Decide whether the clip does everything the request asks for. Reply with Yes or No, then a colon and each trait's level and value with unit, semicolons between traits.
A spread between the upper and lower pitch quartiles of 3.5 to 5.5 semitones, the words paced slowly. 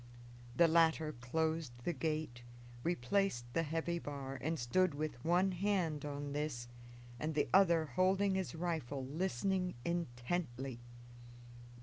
Yes: average, 4.0 semitones; slow, 120 wpm